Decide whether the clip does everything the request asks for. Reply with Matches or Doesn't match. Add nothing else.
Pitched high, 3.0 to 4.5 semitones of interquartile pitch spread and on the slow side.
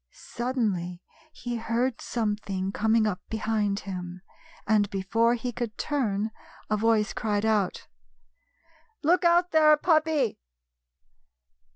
Matches